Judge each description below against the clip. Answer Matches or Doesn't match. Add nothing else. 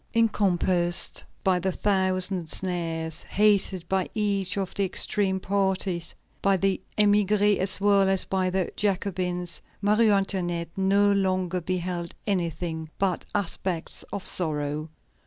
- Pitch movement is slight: Matches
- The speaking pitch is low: Doesn't match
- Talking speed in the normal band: Doesn't match